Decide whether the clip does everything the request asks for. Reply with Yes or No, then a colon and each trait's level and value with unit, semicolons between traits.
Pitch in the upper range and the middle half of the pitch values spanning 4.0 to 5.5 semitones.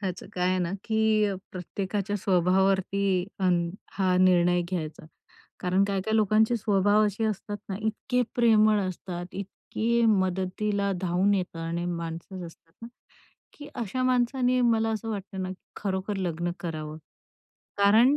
No: high, 195 Hz; average, 3.1 semitones